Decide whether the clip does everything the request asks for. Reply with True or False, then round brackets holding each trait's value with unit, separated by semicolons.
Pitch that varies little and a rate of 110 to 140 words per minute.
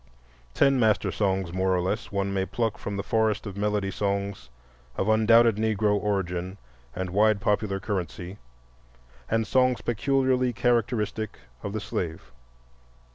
True (2.3 semitones; 135 wpm)